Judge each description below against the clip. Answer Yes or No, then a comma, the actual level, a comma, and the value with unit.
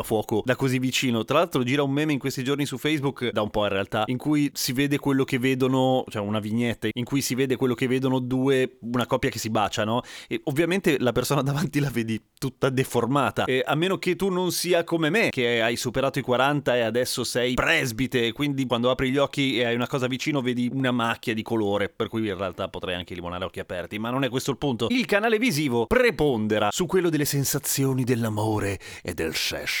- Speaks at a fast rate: Yes, fast, 225 wpm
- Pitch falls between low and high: No, low, 130 Hz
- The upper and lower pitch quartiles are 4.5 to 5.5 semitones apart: No, average, 3.4 semitones